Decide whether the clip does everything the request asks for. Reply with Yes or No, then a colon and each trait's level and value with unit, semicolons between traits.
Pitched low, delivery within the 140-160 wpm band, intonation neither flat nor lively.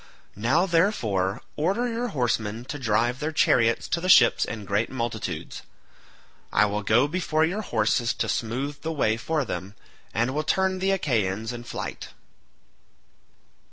No: low, 125 Hz; average, 150 wpm; wide, 6.6 semitones